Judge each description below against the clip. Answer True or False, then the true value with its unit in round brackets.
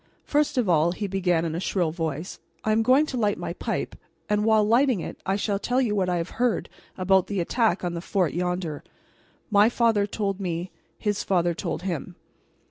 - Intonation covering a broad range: False (3.8 semitones)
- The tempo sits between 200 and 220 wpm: True (205 wpm)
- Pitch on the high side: True (195 Hz)